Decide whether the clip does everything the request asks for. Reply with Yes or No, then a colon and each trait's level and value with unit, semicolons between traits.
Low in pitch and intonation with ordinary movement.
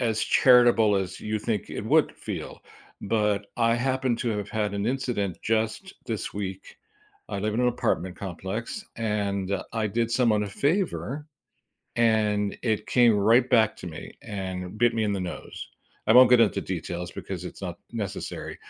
Yes: low, 110 Hz; average, 3.0 semitones